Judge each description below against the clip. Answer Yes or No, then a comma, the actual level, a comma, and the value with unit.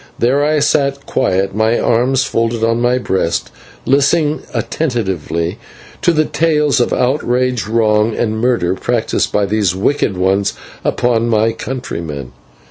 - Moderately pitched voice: No, low, 115 Hz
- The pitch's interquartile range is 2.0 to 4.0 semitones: No, average, 4.8 semitones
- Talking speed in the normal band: No, slow, 130 wpm